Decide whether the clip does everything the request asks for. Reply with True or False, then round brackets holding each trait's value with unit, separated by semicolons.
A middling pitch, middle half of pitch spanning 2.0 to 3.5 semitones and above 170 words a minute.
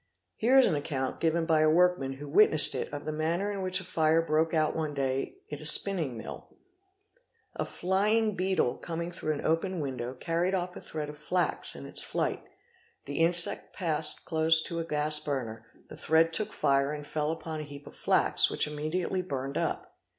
True (160 Hz; 3.1 semitones; 200 wpm)